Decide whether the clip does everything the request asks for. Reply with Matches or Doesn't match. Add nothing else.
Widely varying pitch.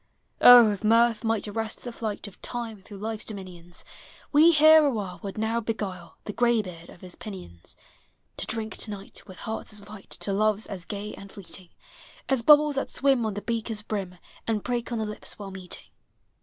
Doesn't match